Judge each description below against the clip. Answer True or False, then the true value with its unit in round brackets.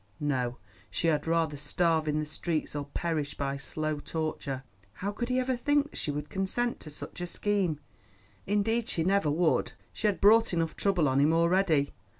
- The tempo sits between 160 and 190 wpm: True (185 wpm)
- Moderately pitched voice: True (165 Hz)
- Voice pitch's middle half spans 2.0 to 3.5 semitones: False (5.1 semitones)